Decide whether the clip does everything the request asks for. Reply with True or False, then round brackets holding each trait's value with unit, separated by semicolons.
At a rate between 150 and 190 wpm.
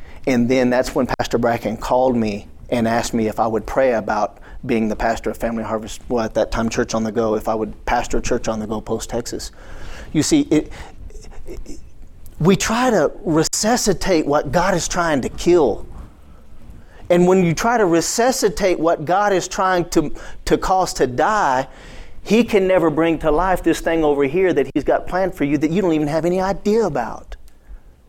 False (200 wpm)